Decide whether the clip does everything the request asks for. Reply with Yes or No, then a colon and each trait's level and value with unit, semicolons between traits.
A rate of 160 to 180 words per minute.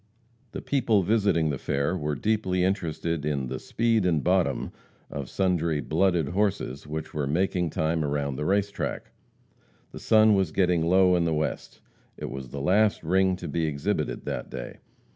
Yes: average, 170 wpm